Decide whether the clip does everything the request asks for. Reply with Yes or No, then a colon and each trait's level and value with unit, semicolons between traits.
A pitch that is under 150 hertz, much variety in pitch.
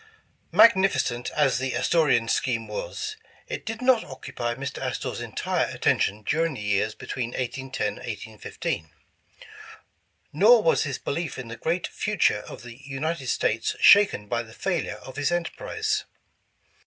Yes: low, 135 Hz; wide, 6.9 semitones